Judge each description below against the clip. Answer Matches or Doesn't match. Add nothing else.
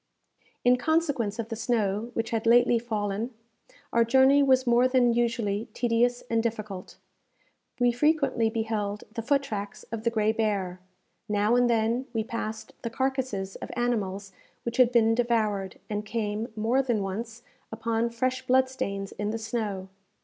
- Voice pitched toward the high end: Matches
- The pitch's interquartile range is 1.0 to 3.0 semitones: Matches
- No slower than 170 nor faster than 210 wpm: Doesn't match